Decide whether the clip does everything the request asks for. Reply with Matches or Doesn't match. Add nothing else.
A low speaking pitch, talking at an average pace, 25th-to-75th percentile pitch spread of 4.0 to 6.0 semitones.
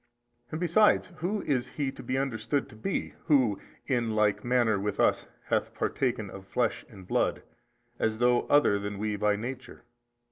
Matches